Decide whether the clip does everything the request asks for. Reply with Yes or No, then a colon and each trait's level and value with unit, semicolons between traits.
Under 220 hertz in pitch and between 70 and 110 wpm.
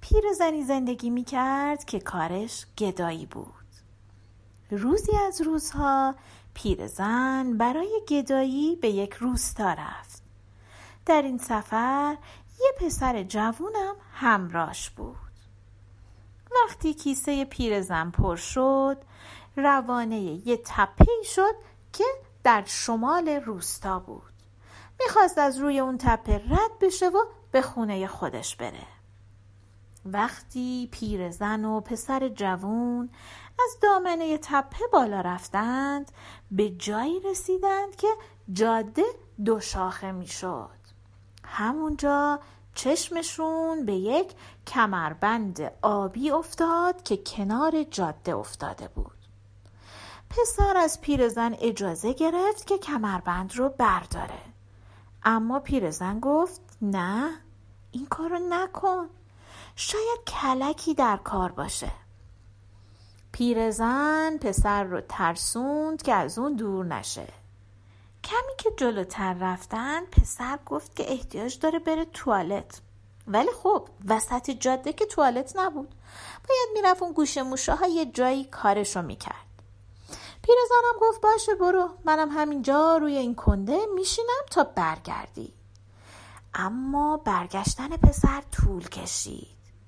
No: high, 240 Hz; slow, 105 wpm